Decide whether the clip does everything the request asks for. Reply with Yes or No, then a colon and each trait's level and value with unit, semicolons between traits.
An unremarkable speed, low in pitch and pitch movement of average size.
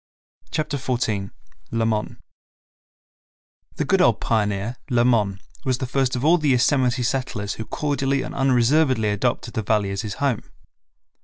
Yes: average, 145 wpm; low, 120 Hz; average, 3.8 semitones